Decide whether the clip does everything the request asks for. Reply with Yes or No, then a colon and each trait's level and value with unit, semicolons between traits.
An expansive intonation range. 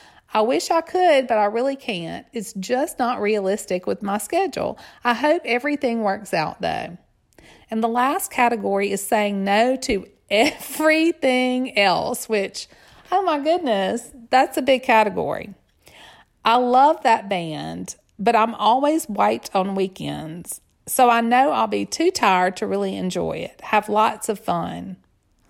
No: average, 5.0 semitones